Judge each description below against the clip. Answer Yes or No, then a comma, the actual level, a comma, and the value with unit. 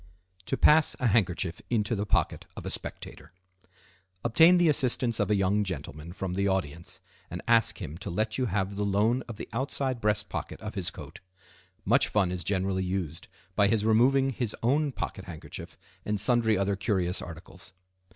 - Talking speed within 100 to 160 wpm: No, average, 175 wpm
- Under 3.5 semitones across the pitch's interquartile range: No, average, 4.0 semitones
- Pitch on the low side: Yes, low, 100 Hz